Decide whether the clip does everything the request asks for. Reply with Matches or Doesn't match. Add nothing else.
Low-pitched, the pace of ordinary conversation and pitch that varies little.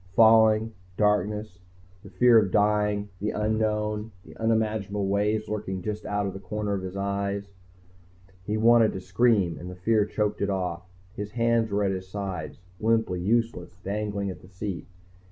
Matches